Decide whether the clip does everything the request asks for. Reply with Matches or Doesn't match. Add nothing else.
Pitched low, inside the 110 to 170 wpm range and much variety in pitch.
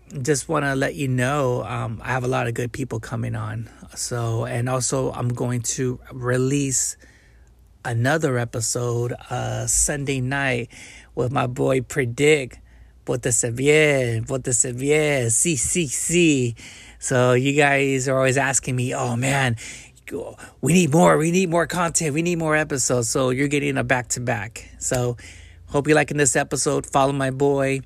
Doesn't match